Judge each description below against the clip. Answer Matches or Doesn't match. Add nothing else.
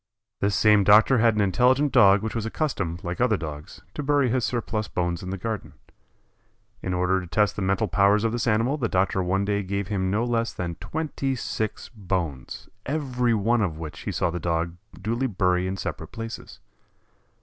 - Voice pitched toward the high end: Doesn't match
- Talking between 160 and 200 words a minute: Matches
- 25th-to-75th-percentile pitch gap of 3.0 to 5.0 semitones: Matches